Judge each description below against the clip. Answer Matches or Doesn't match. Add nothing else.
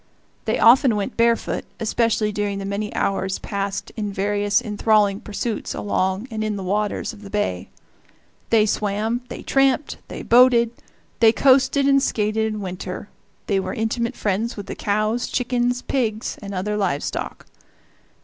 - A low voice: Doesn't match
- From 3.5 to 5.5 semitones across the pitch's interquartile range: Doesn't match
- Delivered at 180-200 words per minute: Doesn't match